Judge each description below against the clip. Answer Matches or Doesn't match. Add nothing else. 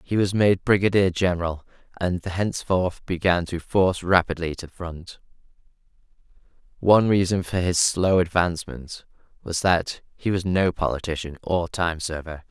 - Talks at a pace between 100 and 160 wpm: Matches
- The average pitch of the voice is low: Matches